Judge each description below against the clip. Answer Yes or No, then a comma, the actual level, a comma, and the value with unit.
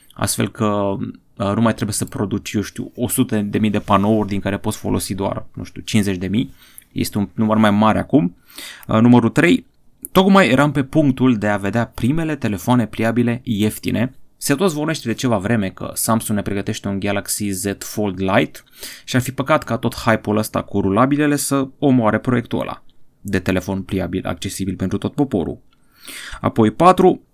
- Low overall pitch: Yes, low, 110 Hz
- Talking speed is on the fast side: Yes, fast, 180 wpm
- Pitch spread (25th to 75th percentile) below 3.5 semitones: No, average, 3.8 semitones